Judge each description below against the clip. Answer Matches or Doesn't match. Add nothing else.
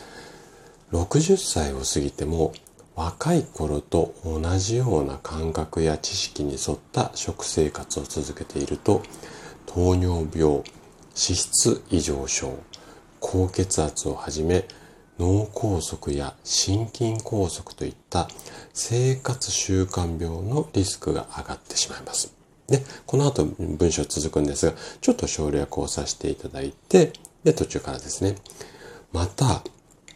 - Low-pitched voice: Matches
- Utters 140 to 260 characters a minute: Matches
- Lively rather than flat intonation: Doesn't match